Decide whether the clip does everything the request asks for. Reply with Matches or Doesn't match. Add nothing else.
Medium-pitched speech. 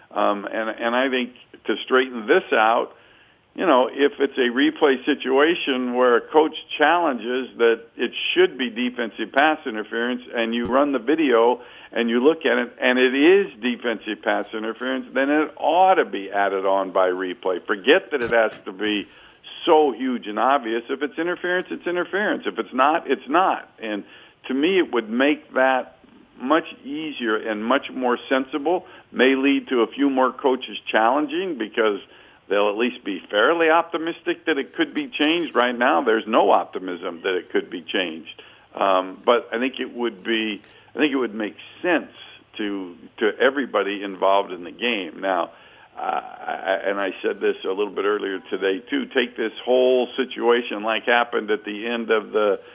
Doesn't match